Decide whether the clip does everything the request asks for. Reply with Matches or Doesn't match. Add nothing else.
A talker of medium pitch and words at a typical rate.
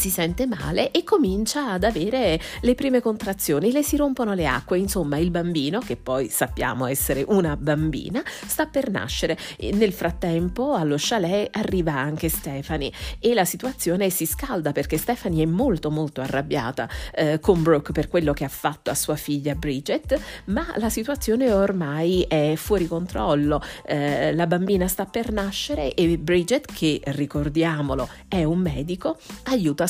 Matches